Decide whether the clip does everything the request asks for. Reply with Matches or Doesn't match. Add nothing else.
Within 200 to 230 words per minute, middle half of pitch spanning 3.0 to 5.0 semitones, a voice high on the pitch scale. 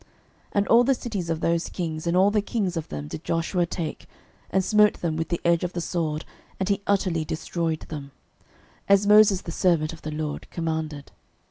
Doesn't match